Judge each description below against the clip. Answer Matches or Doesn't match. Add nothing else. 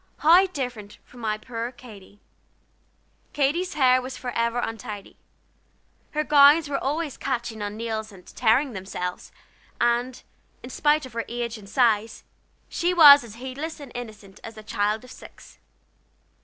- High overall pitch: Matches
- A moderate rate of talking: Matches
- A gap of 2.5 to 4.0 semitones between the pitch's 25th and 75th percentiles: Doesn't match